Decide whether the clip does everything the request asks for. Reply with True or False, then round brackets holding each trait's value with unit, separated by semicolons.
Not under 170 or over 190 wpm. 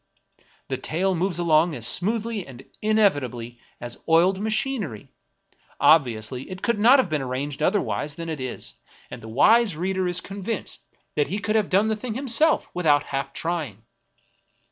True (175 wpm)